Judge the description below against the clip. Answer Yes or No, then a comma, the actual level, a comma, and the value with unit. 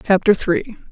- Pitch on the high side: Yes, high, 195 Hz